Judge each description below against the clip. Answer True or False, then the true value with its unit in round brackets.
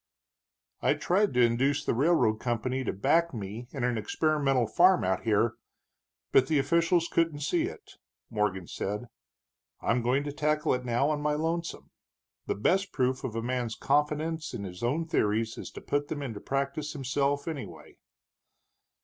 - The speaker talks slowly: False (165 wpm)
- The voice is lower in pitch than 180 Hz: True (135 Hz)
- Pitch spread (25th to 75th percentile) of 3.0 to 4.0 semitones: False (4.7 semitones)